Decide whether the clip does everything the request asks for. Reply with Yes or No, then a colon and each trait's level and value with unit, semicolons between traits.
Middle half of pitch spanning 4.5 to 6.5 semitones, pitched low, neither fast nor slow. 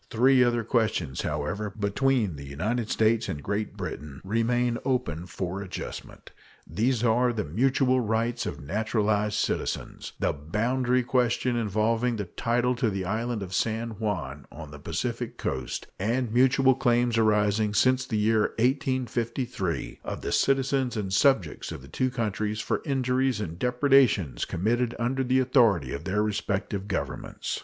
No: average, 3.7 semitones; low, 115 Hz; average, 150 wpm